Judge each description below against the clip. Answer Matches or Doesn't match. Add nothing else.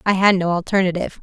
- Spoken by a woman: Matches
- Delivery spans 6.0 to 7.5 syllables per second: Matches